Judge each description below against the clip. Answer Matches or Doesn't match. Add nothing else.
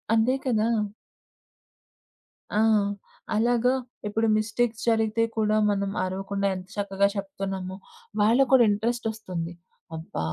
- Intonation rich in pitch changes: Doesn't match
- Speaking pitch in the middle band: Doesn't match